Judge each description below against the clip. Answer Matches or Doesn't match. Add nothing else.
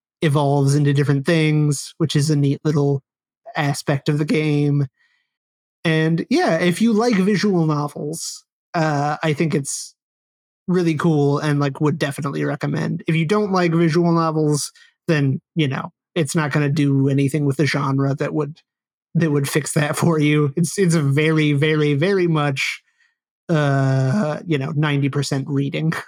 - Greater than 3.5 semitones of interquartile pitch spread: Doesn't match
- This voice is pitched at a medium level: Matches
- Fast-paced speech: Doesn't match